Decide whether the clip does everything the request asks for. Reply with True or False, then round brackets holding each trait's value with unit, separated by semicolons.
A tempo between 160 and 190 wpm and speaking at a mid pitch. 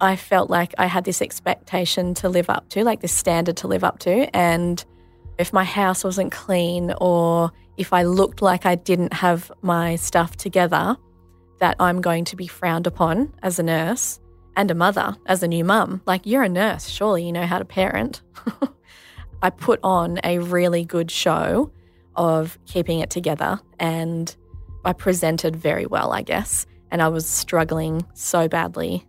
True (175 wpm; 175 Hz)